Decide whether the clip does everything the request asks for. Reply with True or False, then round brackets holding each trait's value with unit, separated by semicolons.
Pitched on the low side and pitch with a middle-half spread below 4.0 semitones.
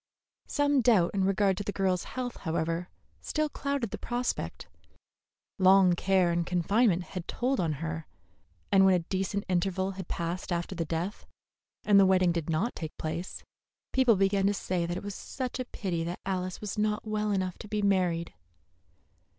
False (190 Hz; 3.2 semitones)